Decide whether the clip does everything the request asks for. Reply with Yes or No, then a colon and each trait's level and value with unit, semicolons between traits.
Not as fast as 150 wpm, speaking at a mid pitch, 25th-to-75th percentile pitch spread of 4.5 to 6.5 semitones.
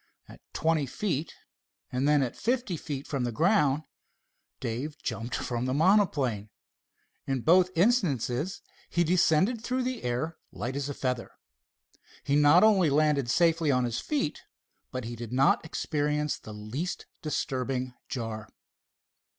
Yes: average, 140 wpm; medium, 145 Hz; average, 5.2 semitones